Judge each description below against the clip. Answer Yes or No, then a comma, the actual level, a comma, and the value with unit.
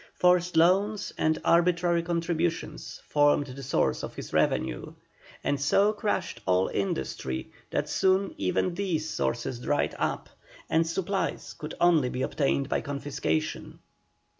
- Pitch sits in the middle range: Yes, medium, 160 Hz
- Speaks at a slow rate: Yes, slow, 130 wpm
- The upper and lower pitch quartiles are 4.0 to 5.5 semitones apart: Yes, average, 4.5 semitones